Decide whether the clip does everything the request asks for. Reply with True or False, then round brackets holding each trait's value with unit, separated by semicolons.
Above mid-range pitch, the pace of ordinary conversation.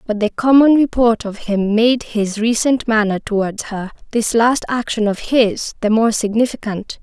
True (225 Hz; 170 wpm)